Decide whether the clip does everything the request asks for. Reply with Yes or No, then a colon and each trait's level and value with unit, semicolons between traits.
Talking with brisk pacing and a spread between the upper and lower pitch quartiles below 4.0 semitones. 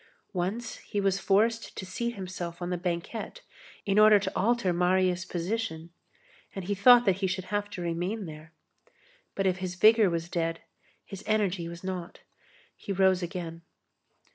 No: average, 165 wpm; average, 2.8 semitones